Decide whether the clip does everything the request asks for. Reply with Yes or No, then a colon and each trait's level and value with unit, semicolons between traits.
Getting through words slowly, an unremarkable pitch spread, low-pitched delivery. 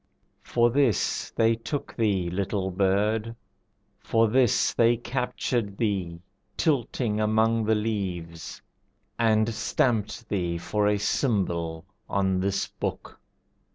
Yes: slow, 110 wpm; average, 3.1 semitones; low, 105 Hz